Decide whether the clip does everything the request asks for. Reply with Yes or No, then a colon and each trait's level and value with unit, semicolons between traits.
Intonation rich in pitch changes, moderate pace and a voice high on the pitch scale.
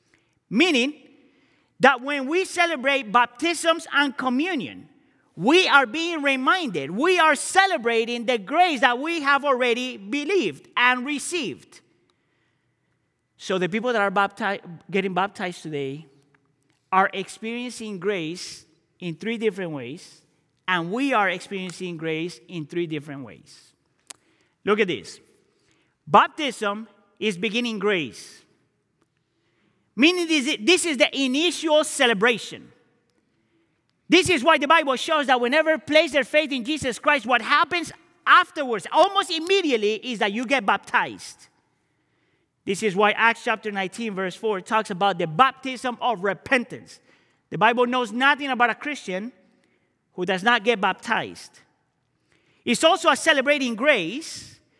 No: wide, 7.0 semitones; slow, 130 wpm; high, 245 Hz